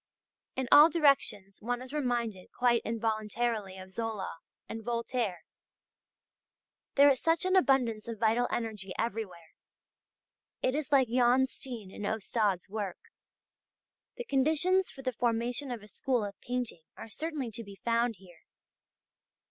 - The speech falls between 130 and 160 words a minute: Yes, average, 140 wpm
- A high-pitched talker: Yes, high, 235 Hz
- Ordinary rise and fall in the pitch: Yes, average, 3.7 semitones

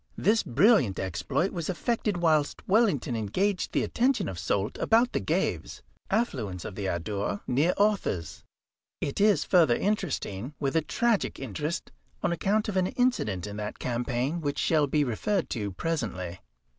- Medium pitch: Yes, medium, 150 Hz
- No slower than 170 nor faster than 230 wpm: No, average, 155 wpm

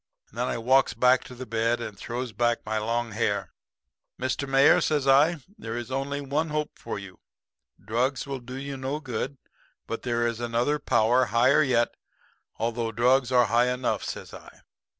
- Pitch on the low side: Yes, low, 125 Hz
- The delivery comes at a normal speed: Yes, average, 180 wpm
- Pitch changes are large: No, narrow, 2.5 semitones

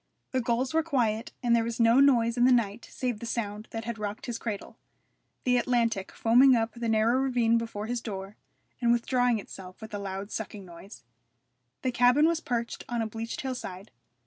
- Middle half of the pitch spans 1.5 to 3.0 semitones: Yes, narrow, 2.4 semitones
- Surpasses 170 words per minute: Yes, average, 195 wpm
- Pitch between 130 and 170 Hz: No, high, 230 Hz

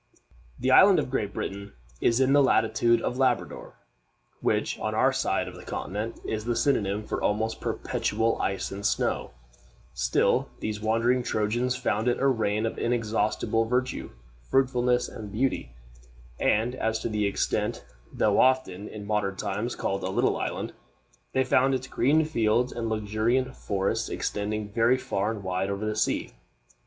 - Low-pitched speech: Yes, low, 110 Hz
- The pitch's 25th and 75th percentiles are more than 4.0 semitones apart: No, average, 3.3 semitones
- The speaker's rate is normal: Yes, average, 160 wpm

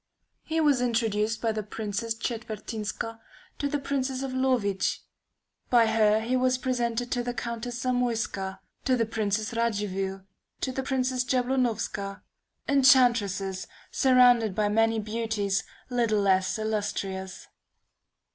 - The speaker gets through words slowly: Yes, slow, 120 wpm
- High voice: Yes, high, 225 Hz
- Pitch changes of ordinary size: Yes, average, 3.3 semitones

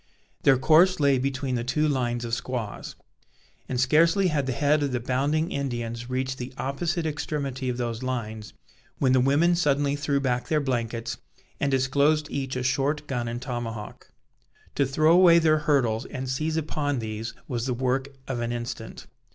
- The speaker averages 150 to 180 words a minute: Yes, average, 175 wpm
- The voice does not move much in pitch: No, average, 3.3 semitones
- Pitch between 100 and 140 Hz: Yes, low, 135 Hz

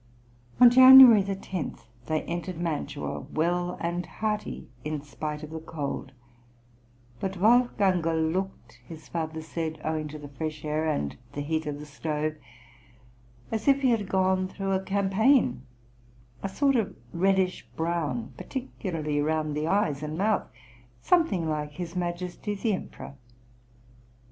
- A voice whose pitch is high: No, medium, 170 Hz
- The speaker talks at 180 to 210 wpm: No, average, 140 wpm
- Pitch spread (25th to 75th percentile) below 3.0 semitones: No, average, 4.2 semitones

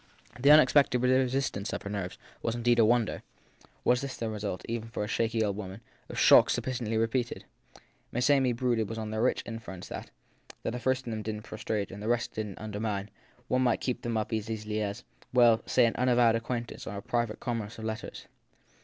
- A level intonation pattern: Yes, narrow, 2.3 semitones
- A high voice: No, low, 115 Hz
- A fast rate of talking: Yes, fast, 215 wpm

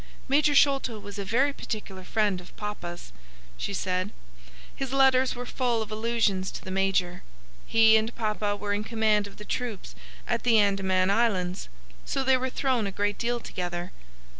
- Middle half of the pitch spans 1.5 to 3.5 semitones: No, average, 3.9 semitones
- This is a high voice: Yes, high, 215 Hz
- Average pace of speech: Yes, average, 170 wpm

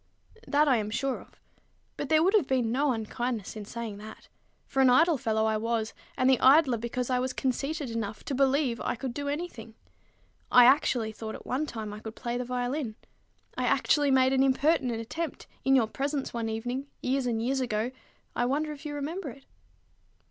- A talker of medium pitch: No, very high, 255 Hz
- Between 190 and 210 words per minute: Yes, average, 200 wpm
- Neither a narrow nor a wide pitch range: Yes, average, 3.6 semitones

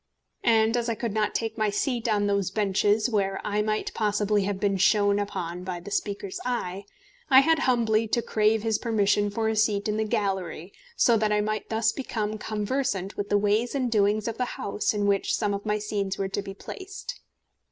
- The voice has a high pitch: Yes, high, 210 Hz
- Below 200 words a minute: No, fast, 205 wpm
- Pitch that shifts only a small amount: Yes, narrow, 1.8 semitones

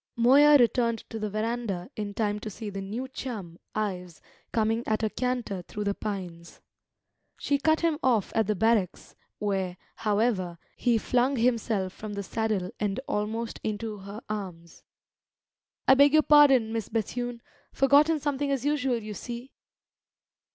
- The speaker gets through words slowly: No, average, 150 wpm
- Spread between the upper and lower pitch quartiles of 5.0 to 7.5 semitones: No, average, 3.6 semitones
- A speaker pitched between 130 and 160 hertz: No, high, 220 Hz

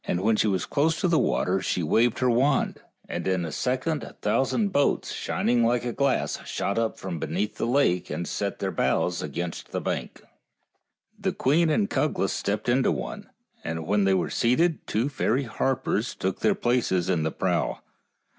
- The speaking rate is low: No, average, 180 wpm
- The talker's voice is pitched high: No, low, 115 Hz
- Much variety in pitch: Yes, wide, 6.6 semitones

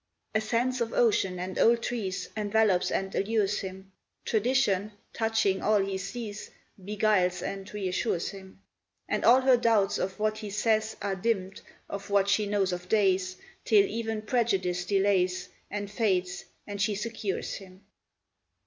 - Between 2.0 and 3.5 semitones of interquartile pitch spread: Yes, narrow, 2.5 semitones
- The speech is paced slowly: No, average, 150 wpm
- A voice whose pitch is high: Yes, high, 205 Hz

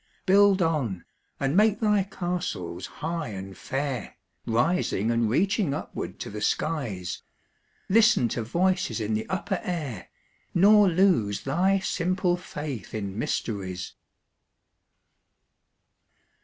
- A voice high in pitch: No, medium, 155 Hz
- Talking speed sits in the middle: No, slow, 110 wpm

